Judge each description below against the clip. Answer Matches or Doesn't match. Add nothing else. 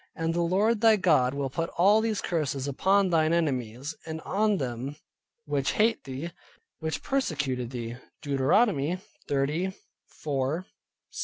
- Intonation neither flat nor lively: Doesn't match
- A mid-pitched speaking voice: Matches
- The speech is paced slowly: Matches